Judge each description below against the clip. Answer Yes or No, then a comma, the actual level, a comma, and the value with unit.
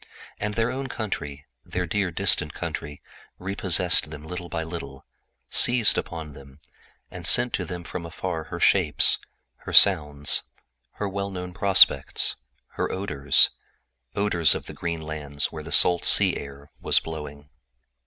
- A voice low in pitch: Yes, very low, 85 Hz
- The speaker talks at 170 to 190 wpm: No, average, 145 wpm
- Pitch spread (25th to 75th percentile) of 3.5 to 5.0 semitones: Yes, average, 4.6 semitones